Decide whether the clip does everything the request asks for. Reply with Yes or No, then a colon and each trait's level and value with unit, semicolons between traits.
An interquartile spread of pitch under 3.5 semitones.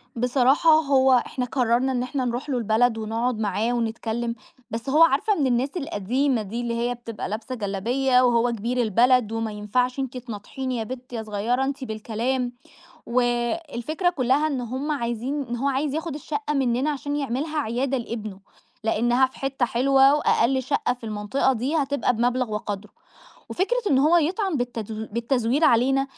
Yes: average, 2.9 semitones